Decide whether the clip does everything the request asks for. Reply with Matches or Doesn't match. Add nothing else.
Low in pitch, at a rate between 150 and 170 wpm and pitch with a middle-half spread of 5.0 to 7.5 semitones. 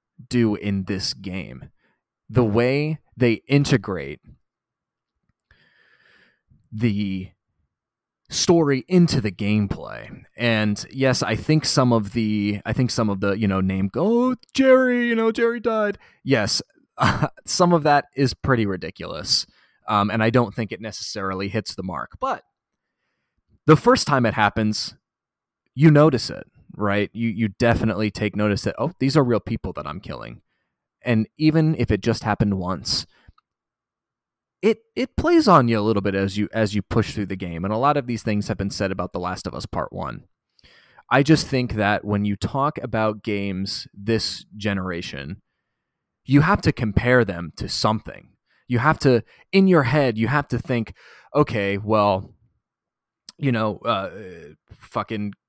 Matches